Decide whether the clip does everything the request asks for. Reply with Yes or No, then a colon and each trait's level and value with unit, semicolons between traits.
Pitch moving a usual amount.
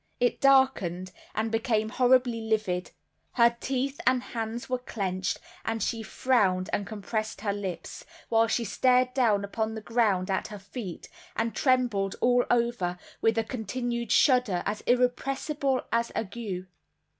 Yes: average, 3.6 semitones